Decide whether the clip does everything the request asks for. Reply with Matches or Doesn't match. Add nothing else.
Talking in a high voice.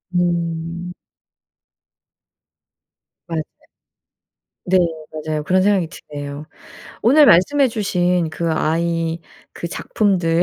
Doesn't match